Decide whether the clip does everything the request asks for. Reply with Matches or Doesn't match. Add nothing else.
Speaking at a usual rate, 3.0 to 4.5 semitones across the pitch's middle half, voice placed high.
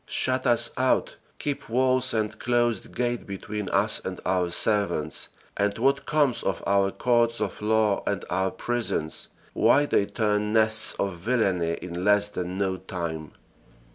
Doesn't match